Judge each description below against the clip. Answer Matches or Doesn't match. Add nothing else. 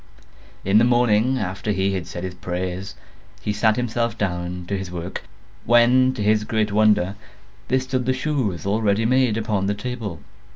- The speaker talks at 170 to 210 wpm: Matches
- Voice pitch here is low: Matches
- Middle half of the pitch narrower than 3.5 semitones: Doesn't match